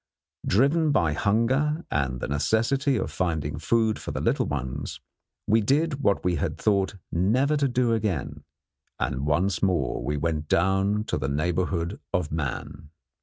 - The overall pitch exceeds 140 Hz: No, very low, 95 Hz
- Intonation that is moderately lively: No, wide, 7.4 semitones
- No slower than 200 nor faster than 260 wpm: No, average, 150 wpm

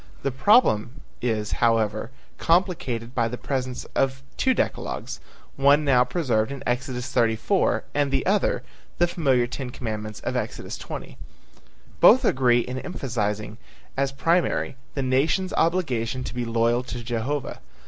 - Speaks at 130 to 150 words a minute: Yes, average, 140 wpm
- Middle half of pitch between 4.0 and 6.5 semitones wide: No, average, 3.3 semitones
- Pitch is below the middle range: Yes, low, 130 Hz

